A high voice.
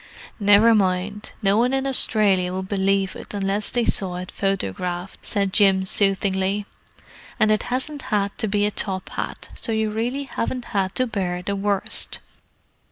Yes: high, 200 Hz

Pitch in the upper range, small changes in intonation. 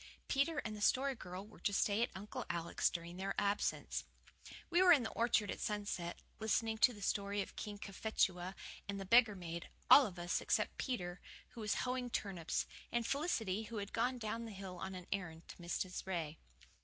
No: high, 205 Hz; average, 4.0 semitones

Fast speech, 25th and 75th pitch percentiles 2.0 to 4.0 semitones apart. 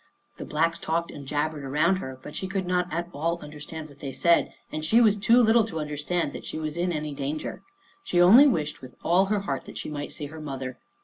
Yes: fast, 235 wpm; average, 3.4 semitones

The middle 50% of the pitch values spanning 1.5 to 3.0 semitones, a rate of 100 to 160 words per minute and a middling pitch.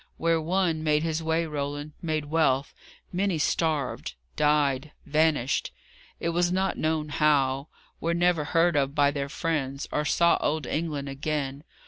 Yes: narrow, 2.5 semitones; average, 145 wpm; medium, 155 Hz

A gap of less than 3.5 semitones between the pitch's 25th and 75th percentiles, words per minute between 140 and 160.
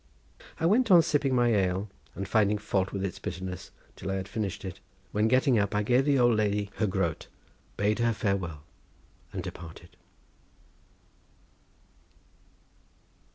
No: average, 4.1 semitones; average, 145 wpm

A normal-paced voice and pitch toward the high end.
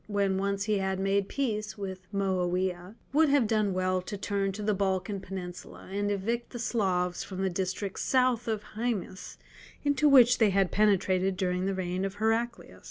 Yes: average, 175 wpm; high, 195 Hz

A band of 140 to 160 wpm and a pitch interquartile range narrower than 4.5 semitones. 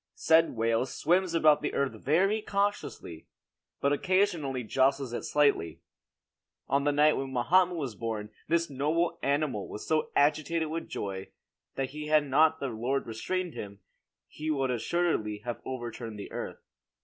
No: average, 150 wpm; average, 5.1 semitones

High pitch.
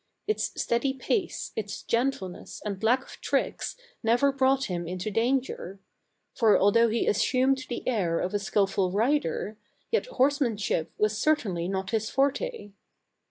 Yes: high, 225 Hz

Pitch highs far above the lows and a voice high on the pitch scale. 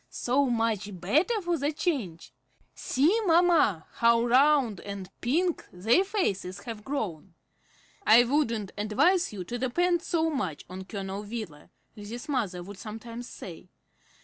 Yes: wide, 7.0 semitones; high, 230 Hz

